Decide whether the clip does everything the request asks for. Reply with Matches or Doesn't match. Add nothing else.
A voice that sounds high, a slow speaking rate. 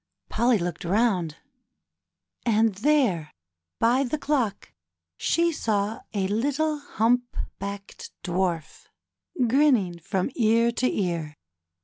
Matches